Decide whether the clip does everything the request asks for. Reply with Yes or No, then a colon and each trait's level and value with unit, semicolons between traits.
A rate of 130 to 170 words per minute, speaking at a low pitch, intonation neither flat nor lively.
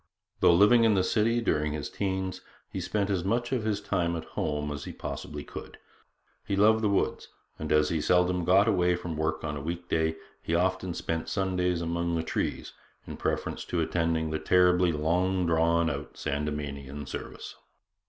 No: average, 185 wpm; very low, 85 Hz; average, 3.2 semitones